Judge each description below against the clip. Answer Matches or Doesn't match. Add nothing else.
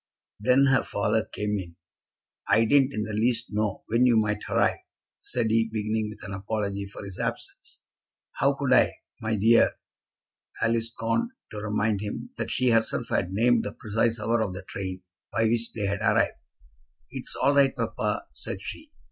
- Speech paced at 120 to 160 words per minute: Doesn't match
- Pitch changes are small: Matches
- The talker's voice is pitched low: Matches